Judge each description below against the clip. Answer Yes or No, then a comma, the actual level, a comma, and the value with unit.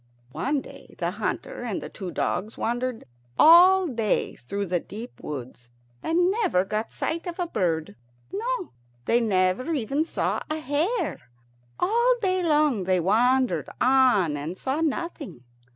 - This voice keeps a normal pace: Yes, average, 150 wpm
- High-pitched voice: Yes, very high, 255 Hz